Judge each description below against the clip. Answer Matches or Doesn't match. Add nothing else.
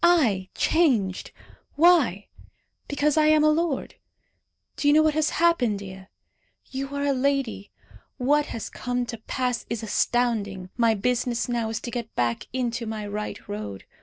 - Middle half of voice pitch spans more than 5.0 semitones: Matches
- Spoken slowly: Doesn't match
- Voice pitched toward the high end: Matches